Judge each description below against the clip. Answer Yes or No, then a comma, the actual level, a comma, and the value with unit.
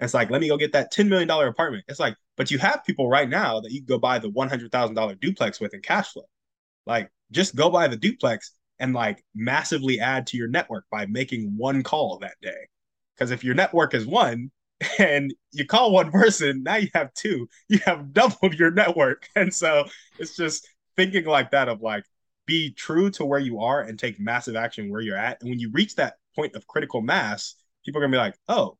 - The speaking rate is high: Yes, fast, 225 wpm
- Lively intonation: Yes, wide, 6.0 semitones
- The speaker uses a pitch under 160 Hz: Yes, medium, 140 Hz